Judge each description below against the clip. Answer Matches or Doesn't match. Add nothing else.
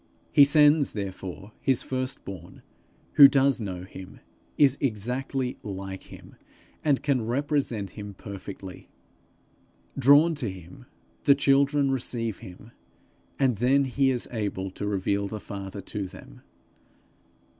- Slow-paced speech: Matches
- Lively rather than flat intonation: Matches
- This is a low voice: Matches